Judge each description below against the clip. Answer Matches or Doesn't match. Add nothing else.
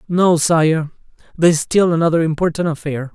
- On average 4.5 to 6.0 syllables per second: Matches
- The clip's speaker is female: Doesn't match